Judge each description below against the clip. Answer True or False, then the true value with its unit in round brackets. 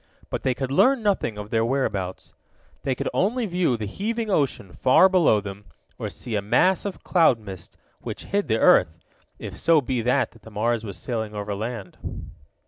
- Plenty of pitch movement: True (8.8 semitones)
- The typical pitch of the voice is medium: False (120 Hz)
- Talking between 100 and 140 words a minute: False (185 wpm)